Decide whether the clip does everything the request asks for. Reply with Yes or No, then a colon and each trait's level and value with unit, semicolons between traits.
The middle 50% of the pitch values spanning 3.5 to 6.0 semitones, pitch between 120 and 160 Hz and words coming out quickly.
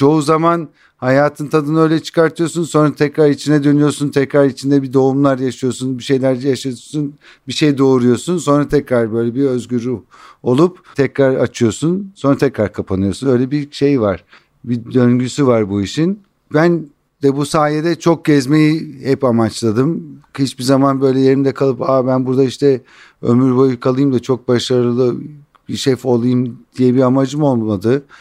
No: average, 2.8 semitones; low, 135 Hz; fast, 155 wpm